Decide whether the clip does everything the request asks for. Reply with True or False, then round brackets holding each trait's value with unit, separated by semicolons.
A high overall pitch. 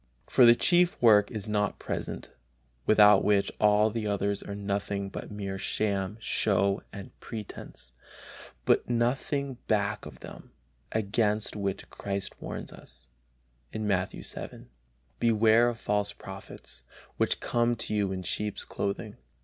False (105 Hz)